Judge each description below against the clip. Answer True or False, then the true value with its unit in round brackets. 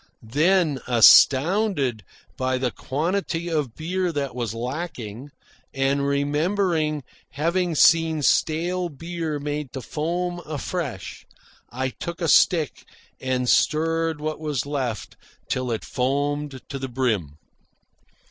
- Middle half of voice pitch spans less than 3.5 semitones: False (4.2 semitones)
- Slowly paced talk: True (115 wpm)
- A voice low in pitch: False (145 Hz)